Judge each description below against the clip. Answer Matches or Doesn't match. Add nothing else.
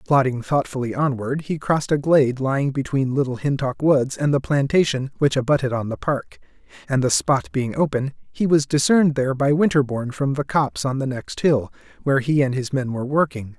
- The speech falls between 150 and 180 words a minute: Doesn't match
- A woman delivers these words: Doesn't match